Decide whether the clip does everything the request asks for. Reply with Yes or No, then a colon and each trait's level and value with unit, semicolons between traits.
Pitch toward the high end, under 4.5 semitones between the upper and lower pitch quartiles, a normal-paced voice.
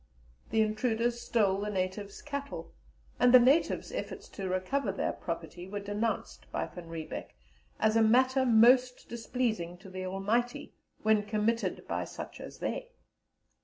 Yes: high, 220 Hz; average, 4.0 semitones; average, 145 wpm